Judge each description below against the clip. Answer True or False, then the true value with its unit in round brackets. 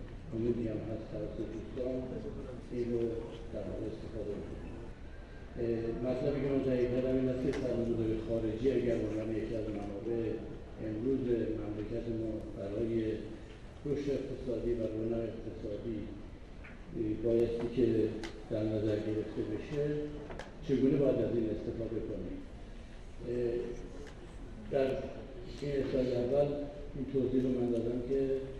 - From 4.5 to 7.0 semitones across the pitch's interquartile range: False (2.8 semitones)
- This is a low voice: True (115 Hz)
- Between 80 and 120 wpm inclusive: True (110 wpm)